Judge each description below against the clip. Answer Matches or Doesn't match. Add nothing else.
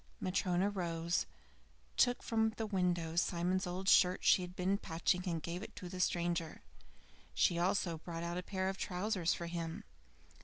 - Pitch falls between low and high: Matches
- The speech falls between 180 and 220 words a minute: Doesn't match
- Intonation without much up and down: Matches